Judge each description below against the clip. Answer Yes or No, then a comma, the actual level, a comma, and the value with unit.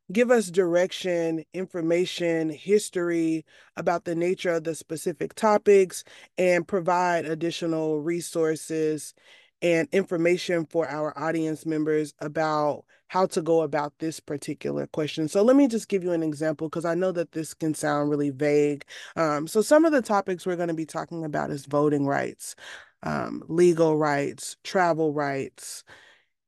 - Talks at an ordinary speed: Yes, average, 150 wpm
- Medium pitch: Yes, medium, 165 Hz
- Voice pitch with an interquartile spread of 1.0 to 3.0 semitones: Yes, average, 2.7 semitones